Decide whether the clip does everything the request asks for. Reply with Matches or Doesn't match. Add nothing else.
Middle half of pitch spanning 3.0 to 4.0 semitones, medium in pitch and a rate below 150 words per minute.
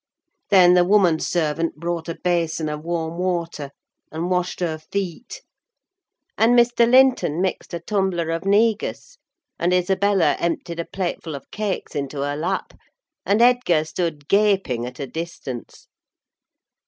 Matches